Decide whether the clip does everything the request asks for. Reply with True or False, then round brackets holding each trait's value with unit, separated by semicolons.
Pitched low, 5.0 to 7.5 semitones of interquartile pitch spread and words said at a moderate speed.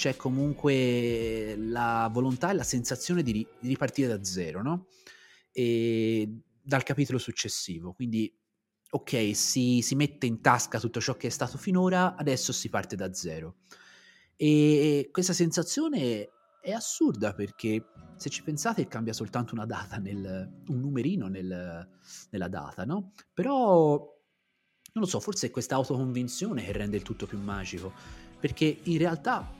True (125 Hz; 5.5 semitones; 145 wpm)